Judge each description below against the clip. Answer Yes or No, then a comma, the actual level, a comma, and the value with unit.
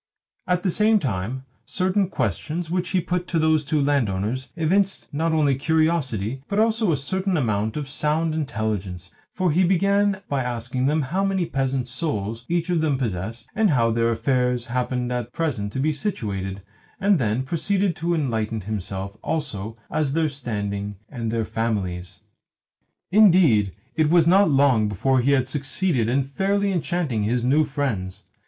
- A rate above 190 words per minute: No, average, 160 wpm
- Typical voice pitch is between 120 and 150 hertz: Yes, low, 135 Hz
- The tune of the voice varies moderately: No, wide, 6.9 semitones